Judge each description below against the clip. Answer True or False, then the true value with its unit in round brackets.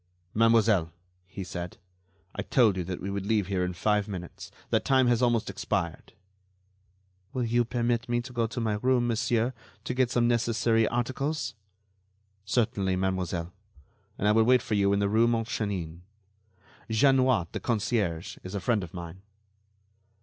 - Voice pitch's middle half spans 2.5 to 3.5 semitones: False (4.0 semitones)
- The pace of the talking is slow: False (160 wpm)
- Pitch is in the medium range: False (110 Hz)